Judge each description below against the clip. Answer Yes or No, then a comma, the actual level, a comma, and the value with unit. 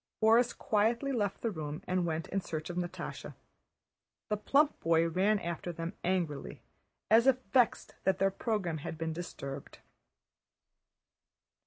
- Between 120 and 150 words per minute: Yes, average, 140 wpm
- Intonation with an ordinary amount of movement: Yes, average, 4.9 semitones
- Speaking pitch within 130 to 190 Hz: Yes, medium, 185 Hz